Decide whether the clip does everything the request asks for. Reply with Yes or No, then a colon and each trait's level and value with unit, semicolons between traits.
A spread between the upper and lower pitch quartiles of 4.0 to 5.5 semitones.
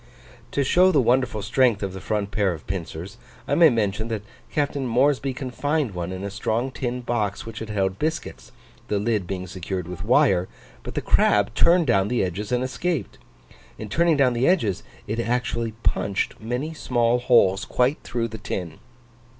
Yes: average, 4.7 semitones